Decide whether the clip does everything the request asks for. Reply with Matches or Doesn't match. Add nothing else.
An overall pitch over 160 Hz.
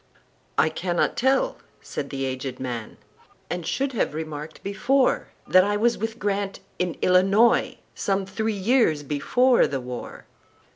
Matches